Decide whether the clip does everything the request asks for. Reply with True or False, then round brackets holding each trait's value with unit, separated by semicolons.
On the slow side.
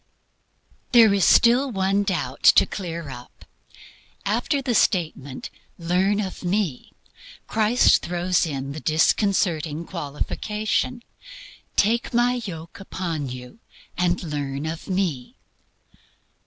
True (105 wpm)